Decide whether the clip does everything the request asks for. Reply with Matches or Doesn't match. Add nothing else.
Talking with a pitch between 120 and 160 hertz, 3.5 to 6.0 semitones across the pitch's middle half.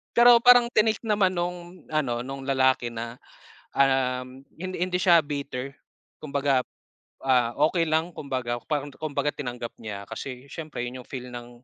Matches